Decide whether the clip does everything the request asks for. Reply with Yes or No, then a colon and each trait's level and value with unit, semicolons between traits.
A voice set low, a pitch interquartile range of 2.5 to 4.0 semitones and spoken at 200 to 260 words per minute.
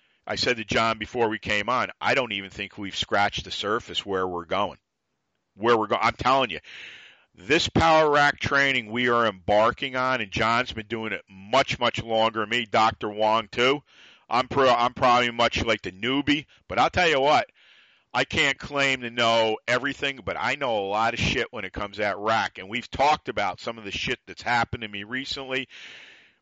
Yes: low, 115 Hz; average, 3.5 semitones; fast, 205 wpm